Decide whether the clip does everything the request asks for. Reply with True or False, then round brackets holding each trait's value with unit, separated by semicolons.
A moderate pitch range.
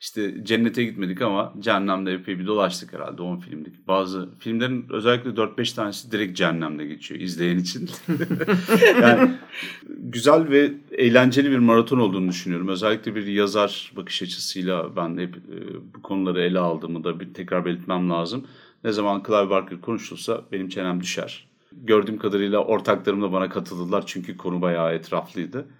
True (4.2 semitones)